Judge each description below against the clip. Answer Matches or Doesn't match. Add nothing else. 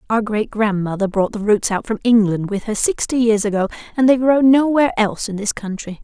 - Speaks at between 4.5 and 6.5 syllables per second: Matches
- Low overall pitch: Doesn't match